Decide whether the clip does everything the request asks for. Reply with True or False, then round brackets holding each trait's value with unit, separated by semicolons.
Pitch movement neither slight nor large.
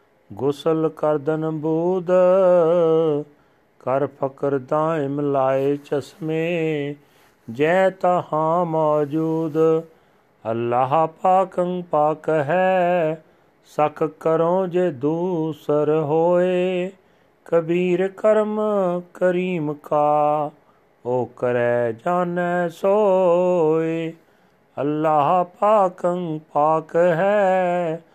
True (3.0 semitones)